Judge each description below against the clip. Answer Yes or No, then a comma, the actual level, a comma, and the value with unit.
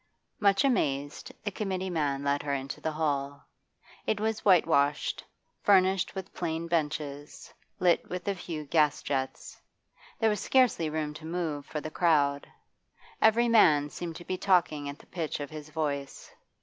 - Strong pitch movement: No, average, 4.4 semitones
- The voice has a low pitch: No, medium, 160 Hz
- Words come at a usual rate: Yes, average, 160 wpm